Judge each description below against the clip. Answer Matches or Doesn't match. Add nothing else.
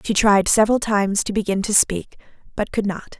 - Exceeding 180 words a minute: Matches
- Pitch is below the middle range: Doesn't match